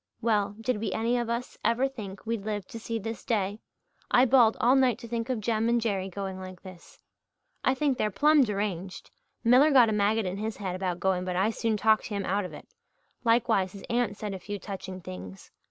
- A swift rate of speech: Yes, fast, 220 wpm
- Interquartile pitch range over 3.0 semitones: Yes, average, 3.4 semitones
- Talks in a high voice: Yes, high, 215 Hz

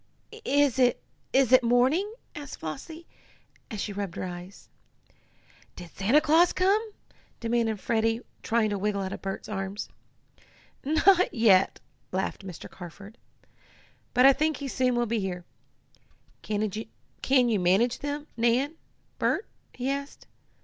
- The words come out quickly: No, slow, 135 wpm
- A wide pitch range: Yes, wide, 5.9 semitones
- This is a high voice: Yes, high, 235 Hz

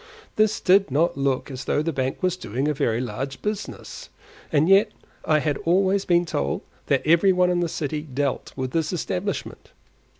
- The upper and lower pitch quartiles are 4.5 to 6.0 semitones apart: Yes, average, 5.0 semitones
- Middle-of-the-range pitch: Yes, medium, 160 Hz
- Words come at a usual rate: Yes, average, 180 wpm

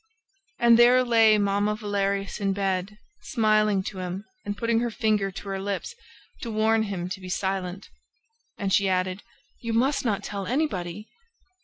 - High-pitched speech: Yes, high, 205 Hz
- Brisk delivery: No, average, 160 wpm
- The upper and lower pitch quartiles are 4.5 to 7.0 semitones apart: No, narrow, 2.6 semitones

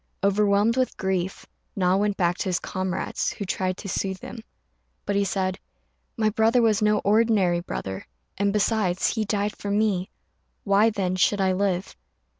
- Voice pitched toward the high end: Yes, high, 200 Hz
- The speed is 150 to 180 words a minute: Yes, average, 165 wpm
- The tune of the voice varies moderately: No, narrow, 2.2 semitones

